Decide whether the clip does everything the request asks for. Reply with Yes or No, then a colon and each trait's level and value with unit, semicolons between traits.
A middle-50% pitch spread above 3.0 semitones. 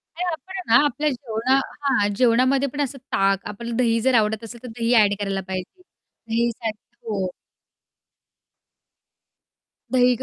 Yes: average, 3.6 semitones